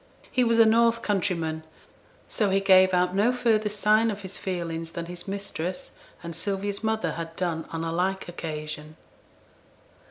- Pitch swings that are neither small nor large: Yes, average, 4.0 semitones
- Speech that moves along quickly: No, average, 160 wpm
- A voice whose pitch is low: No, high, 190 Hz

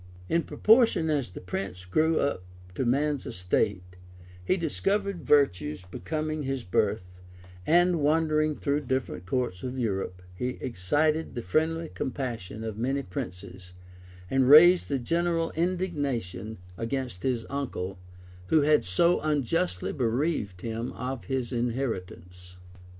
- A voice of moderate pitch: No, low, 130 Hz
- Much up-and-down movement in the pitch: Yes, wide, 8.6 semitones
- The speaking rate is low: Yes, slow, 130 wpm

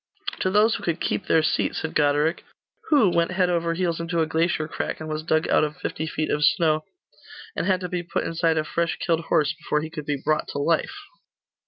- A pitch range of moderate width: No, narrow, 1.8 semitones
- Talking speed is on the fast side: Yes, fast, 225 wpm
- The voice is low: No, medium, 160 Hz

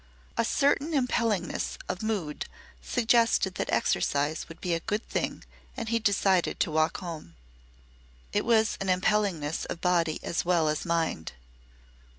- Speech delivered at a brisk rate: No, average, 145 wpm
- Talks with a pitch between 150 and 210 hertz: Yes, medium, 185 Hz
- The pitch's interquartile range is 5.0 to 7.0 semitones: Yes, average, 5.3 semitones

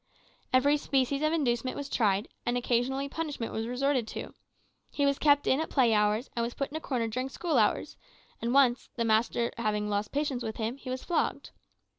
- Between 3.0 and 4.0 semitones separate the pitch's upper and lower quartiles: Yes, average, 3.3 semitones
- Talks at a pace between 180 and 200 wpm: Yes, average, 195 wpm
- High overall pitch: Yes, very high, 255 Hz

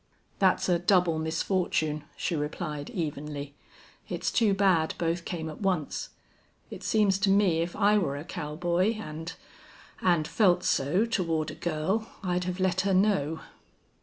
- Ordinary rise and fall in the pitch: Yes, average, 3.6 semitones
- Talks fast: No, average, 150 wpm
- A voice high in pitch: No, medium, 175 Hz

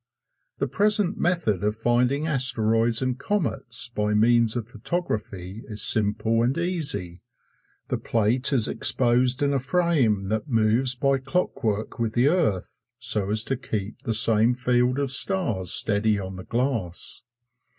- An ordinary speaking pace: Yes, average, 145 wpm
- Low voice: Yes, low, 120 Hz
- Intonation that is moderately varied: Yes, average, 4.1 semitones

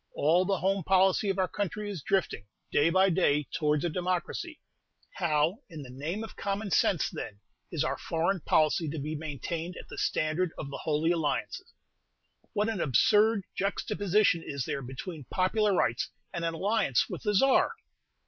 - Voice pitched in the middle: Yes, medium, 175 Hz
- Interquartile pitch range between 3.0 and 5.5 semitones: Yes, average, 4.5 semitones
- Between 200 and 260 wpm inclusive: No, average, 170 wpm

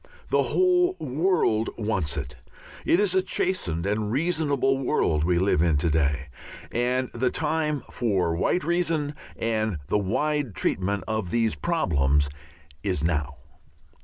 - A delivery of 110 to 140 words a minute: Yes, slow, 135 wpm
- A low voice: Yes, low, 110 Hz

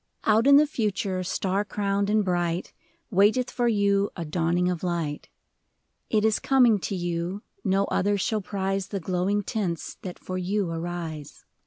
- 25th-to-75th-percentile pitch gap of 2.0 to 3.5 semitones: Yes, average, 2.9 semitones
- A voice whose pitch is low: No, high, 195 Hz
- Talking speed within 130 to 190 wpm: Yes, average, 160 wpm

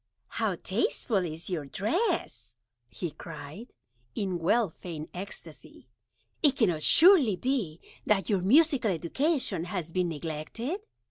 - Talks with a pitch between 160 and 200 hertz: Yes, high, 190 Hz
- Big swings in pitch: Yes, wide, 7.4 semitones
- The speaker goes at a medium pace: No, slow, 120 wpm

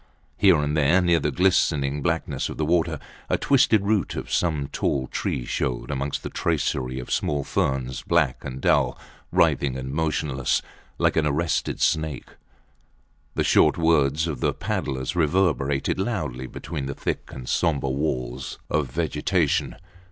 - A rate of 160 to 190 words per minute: No, average, 150 wpm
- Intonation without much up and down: No, average, 3.7 semitones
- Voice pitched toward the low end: Yes, very low, 75 Hz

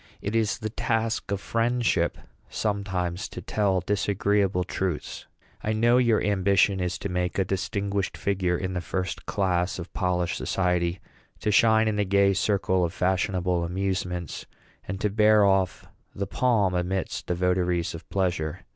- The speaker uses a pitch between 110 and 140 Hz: No, very low, 95 Hz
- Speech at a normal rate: Yes, average, 155 wpm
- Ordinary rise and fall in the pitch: No, narrow, 2.3 semitones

